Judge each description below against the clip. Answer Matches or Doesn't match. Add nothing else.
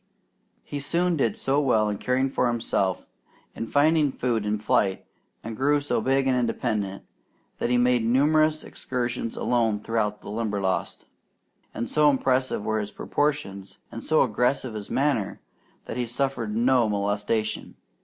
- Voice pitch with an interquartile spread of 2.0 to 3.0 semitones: Doesn't match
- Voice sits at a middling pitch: Doesn't match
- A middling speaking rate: Matches